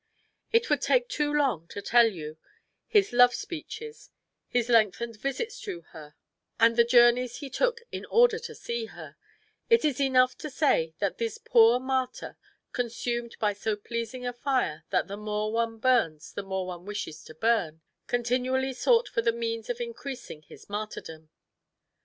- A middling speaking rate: Yes, average, 165 wpm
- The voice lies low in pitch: No, high, 235 Hz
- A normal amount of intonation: Yes, average, 4.2 semitones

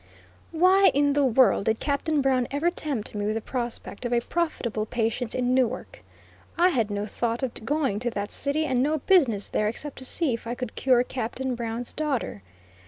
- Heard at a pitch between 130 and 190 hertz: No, very high, 250 Hz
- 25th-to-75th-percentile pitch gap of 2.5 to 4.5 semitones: Yes, average, 4.0 semitones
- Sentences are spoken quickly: No, average, 195 wpm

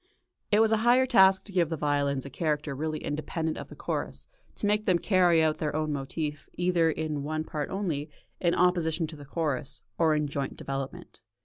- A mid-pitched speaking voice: Yes, medium, 160 Hz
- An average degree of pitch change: Yes, average, 3.4 semitones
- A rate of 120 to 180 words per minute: No, average, 200 wpm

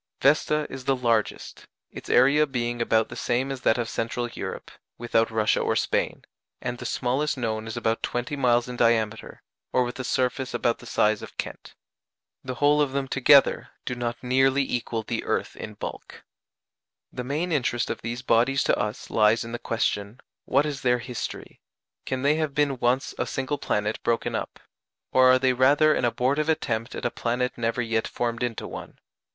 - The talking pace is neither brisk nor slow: Yes, average, 190 wpm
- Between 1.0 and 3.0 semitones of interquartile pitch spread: Yes, narrow, 2.5 semitones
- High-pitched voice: No, low, 125 Hz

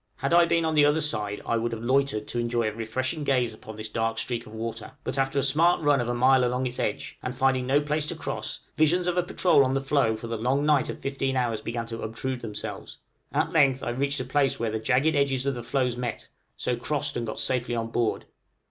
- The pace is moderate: No, fast, 255 wpm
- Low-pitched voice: Yes, low, 130 Hz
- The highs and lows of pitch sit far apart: No, average, 3.4 semitones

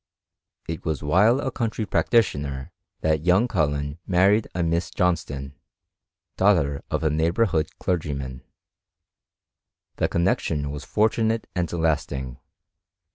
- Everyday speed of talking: No, slow, 125 wpm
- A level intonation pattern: No, average, 5.1 semitones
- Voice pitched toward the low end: Yes, very low, 80 Hz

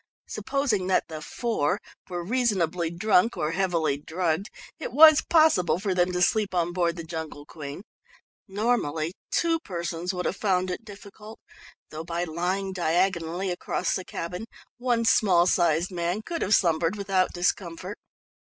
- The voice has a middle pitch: Yes, medium, 180 Hz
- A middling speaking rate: Yes, average, 150 wpm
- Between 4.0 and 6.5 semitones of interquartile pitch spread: No, average, 3.6 semitones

